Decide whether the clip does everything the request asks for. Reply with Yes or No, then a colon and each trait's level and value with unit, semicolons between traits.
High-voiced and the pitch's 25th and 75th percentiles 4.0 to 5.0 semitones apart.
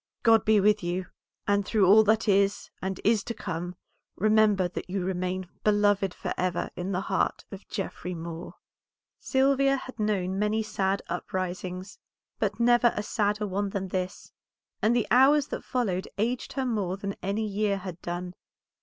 No: high, 200 Hz; average, 2.8 semitones